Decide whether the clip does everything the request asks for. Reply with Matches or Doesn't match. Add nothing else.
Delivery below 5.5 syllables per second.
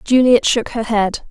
Matches